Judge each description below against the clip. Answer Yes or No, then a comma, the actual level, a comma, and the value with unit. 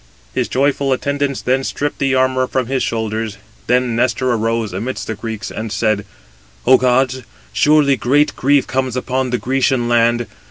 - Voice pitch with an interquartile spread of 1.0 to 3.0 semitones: Yes, narrow, 2.5 semitones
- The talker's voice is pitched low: Yes, low, 125 Hz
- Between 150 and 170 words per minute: Yes, average, 160 wpm